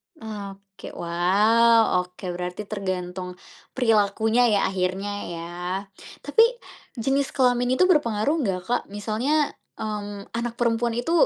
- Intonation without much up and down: No, average, 3.8 semitones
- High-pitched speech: Yes, high, 215 Hz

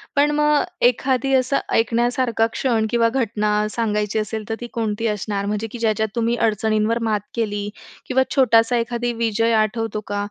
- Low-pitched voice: No, high, 225 Hz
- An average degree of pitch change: No, narrow, 2.1 semitones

